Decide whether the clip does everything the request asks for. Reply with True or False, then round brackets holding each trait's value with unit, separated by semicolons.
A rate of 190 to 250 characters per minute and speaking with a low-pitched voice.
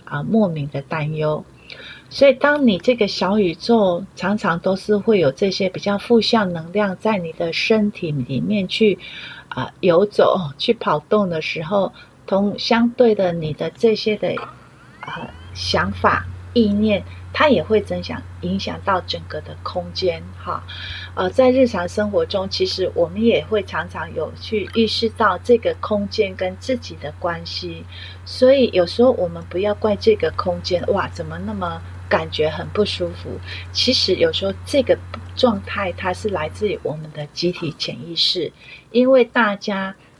False (235 characters per minute; 185 Hz)